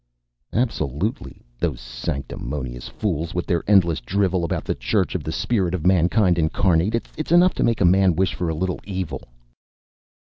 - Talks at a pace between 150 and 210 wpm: Yes, average, 165 wpm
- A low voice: Yes, very low, 90 Hz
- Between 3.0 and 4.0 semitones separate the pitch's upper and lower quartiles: Yes, average, 3.7 semitones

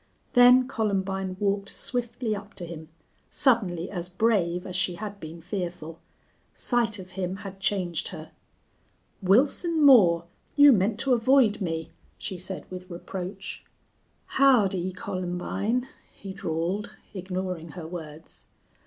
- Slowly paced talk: Yes, slow, 125 wpm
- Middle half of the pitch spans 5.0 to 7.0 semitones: No, average, 3.7 semitones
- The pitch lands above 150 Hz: Yes, high, 190 Hz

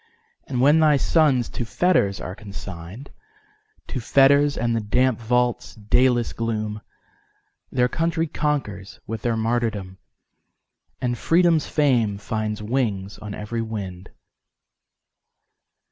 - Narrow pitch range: No, average, 5.2 semitones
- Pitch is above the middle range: No, low, 120 Hz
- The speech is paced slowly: Yes, slow, 100 wpm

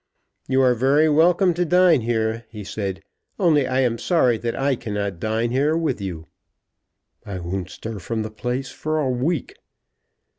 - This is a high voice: No, low, 125 Hz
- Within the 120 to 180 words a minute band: Yes, average, 170 wpm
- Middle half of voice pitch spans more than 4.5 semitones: Yes, wide, 5.5 semitones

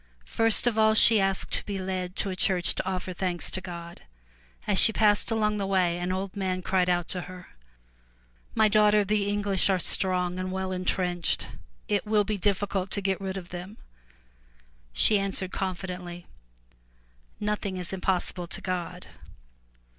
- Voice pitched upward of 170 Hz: Yes, high, 190 Hz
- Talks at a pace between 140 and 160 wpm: No, average, 170 wpm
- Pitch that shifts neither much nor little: No, narrow, 2.1 semitones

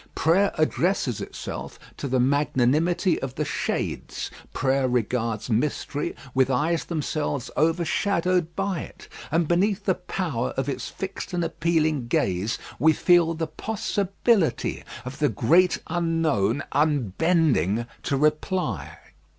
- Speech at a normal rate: No, slow, 120 wpm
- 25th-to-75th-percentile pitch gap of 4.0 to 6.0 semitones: Yes, average, 4.9 semitones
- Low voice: No, medium, 155 Hz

